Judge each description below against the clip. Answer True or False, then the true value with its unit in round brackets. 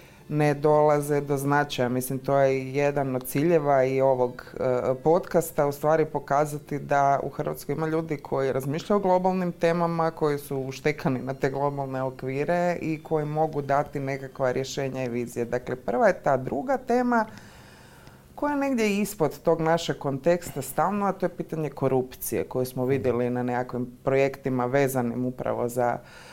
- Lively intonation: False (3.3 semitones)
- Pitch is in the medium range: True (145 Hz)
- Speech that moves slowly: False (160 wpm)